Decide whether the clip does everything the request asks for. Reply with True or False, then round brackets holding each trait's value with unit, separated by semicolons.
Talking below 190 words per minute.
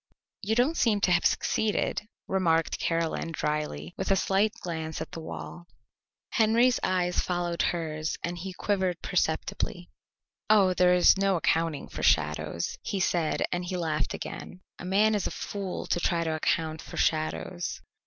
True (160 wpm)